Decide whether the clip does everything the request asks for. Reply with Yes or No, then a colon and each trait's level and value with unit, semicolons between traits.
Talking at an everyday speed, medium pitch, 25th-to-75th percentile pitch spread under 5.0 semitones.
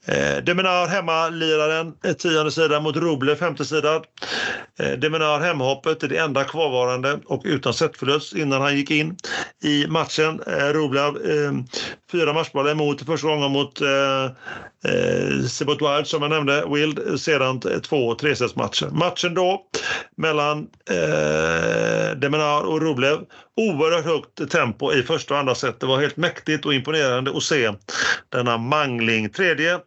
Yes: average, 135 wpm; medium, 150 Hz; narrow, 2.5 semitones